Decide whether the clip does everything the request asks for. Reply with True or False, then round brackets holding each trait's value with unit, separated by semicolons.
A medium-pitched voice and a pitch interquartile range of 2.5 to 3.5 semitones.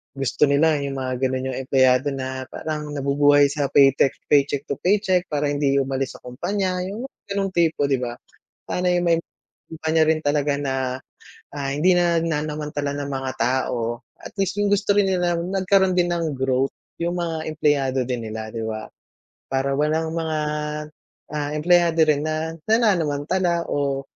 False (150 Hz; 4.0 semitones)